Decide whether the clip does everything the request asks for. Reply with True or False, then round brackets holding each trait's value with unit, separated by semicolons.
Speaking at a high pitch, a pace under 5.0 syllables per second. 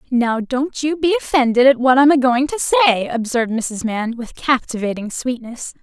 False (250 Hz; 5.1 syllables/s)